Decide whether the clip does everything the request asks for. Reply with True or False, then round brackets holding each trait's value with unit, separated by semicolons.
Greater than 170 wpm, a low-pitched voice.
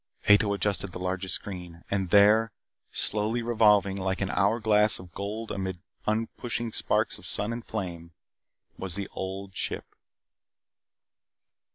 False (135 wpm; 100 Hz)